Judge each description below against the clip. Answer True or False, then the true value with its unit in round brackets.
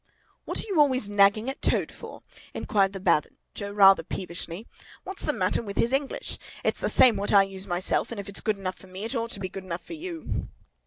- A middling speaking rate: False (225 wpm)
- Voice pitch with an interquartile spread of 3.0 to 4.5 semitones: True (3.6 semitones)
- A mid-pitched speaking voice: False (200 Hz)